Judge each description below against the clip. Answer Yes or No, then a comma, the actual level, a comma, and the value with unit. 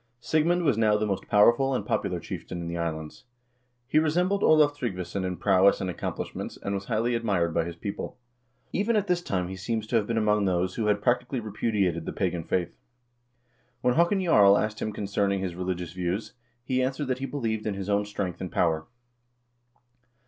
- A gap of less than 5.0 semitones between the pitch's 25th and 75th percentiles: No, average, 5.3 semitones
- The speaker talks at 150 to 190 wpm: No, average, 200 wpm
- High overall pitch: No, low, 105 Hz